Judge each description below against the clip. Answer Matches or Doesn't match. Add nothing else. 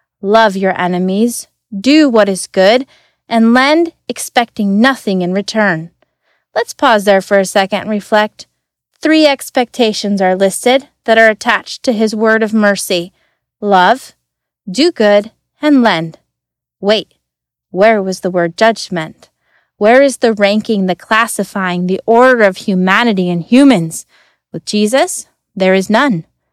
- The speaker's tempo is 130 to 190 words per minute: Matches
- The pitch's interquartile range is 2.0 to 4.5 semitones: Matches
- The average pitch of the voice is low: Doesn't match